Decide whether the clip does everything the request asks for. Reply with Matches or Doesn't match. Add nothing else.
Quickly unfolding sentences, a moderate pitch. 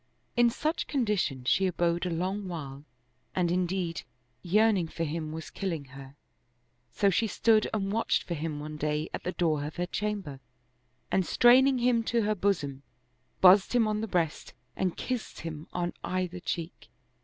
Doesn't match